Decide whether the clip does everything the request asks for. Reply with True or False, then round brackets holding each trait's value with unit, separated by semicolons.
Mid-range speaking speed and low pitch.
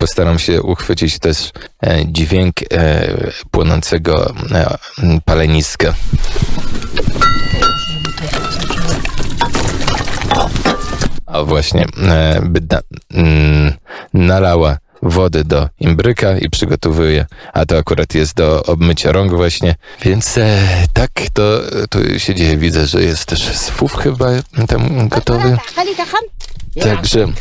False (100 wpm; 85 Hz)